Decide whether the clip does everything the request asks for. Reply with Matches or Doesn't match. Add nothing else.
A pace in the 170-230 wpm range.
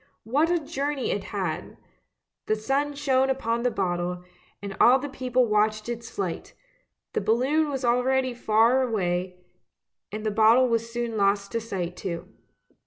Doesn't match